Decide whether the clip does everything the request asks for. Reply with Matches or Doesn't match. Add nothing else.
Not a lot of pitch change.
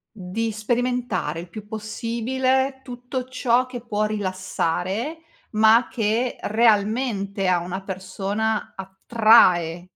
Doesn't match